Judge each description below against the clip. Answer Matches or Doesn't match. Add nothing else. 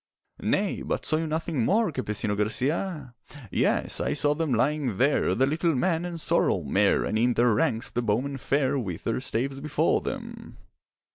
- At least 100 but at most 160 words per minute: Doesn't match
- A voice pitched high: Doesn't match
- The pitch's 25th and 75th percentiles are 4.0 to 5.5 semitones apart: Matches